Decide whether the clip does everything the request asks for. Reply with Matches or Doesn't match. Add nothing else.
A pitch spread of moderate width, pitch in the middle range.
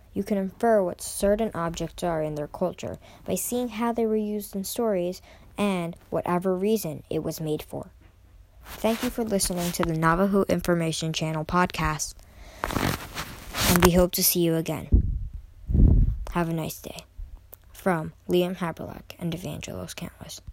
Matches